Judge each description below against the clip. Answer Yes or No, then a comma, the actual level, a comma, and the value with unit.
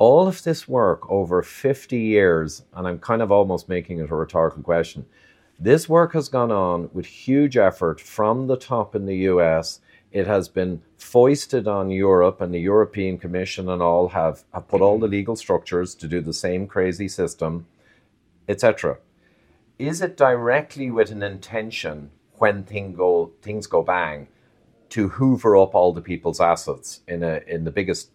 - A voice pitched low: Yes, low, 100 Hz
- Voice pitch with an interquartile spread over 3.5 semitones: Yes, average, 4.7 semitones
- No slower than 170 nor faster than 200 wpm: Yes, average, 175 wpm